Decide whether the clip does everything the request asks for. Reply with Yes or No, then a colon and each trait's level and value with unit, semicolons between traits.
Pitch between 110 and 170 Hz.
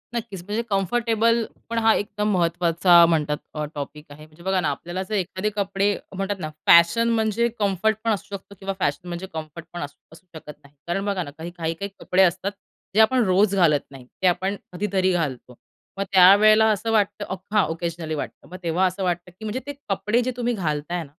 No: medium, 185 Hz